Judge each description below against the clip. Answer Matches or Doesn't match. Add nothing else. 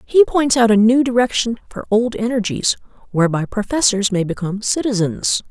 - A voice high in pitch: Matches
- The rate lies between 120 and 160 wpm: Matches